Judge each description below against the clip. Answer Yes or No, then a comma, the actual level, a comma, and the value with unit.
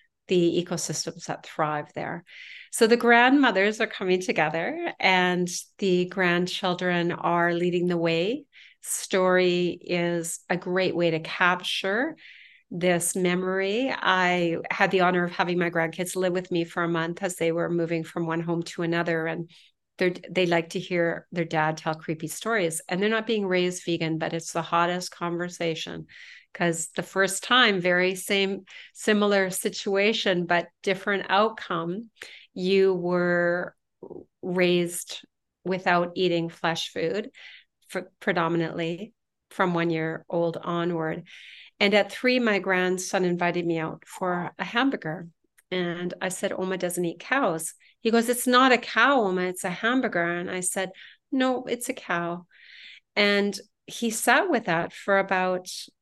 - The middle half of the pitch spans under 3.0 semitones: Yes, narrow, 2.4 semitones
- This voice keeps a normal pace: Yes, average, 150 wpm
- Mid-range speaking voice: Yes, medium, 180 Hz